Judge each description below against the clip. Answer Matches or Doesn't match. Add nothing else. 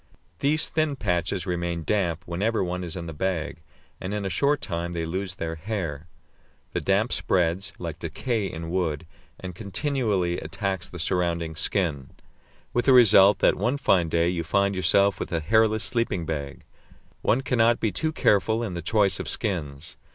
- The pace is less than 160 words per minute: Doesn't match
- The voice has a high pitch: Doesn't match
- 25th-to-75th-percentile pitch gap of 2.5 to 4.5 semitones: Matches